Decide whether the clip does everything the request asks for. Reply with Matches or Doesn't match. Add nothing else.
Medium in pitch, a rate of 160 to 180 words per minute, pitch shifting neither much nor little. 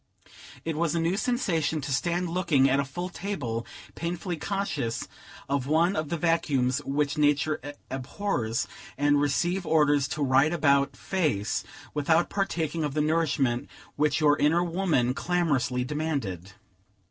Doesn't match